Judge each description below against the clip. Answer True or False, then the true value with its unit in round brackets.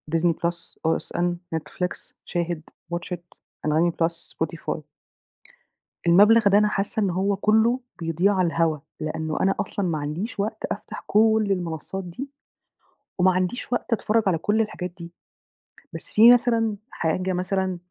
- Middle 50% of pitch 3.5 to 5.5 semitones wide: True (3.8 semitones)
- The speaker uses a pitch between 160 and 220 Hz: True (185 Hz)